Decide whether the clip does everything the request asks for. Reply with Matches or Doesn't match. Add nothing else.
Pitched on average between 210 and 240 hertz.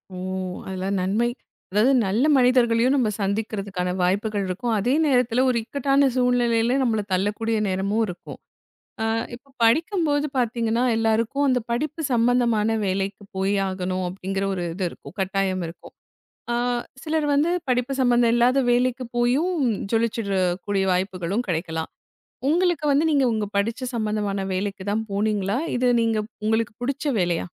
Matches